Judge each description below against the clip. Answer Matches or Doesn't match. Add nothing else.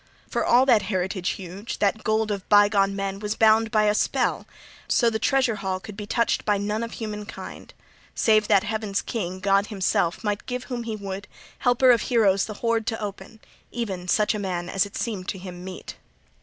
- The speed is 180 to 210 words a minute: Matches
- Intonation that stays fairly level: Matches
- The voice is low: Doesn't match